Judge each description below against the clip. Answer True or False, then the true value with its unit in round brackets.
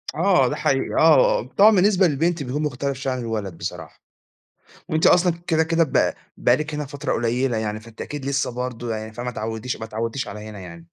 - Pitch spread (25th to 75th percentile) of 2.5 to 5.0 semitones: False (5.4 semitones)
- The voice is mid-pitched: False (125 Hz)